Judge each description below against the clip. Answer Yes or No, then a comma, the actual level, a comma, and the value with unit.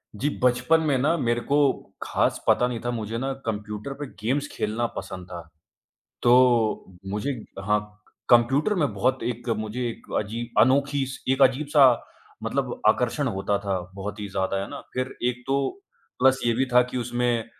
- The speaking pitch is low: Yes, low, 120 Hz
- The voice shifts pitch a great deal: No, average, 4.0 semitones